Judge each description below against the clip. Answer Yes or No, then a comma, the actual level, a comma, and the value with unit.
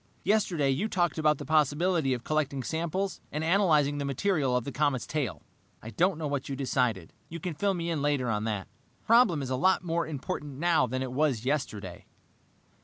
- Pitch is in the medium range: Yes, medium, 145 Hz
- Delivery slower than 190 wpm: No, average, 200 wpm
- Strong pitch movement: No, average, 4.5 semitones